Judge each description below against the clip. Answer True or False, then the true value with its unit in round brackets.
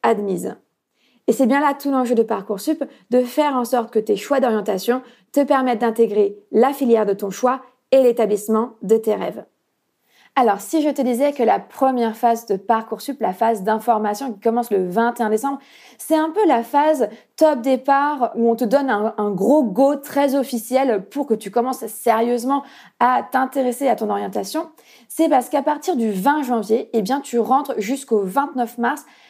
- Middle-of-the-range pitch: False (245 Hz)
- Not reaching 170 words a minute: False (185 wpm)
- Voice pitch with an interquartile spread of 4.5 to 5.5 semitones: False (3.7 semitones)